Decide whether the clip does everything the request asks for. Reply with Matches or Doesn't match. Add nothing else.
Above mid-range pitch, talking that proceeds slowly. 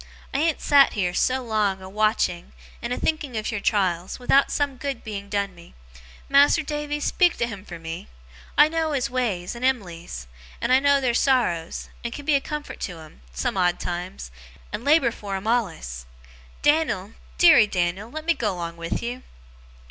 Doesn't match